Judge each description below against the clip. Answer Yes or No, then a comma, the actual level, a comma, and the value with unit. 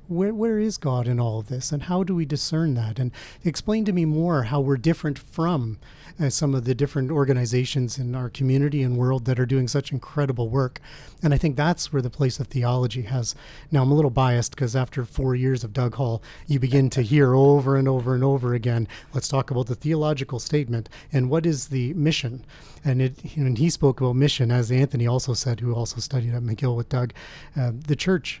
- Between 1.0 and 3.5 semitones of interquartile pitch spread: Yes, average, 2.9 semitones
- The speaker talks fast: Yes, fast, 220 wpm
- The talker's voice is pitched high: No, low, 135 Hz